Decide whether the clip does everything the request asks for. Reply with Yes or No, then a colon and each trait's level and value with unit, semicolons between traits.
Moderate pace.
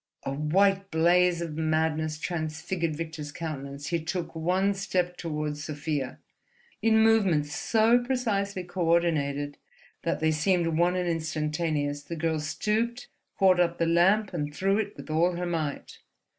Yes: average, 145 wpm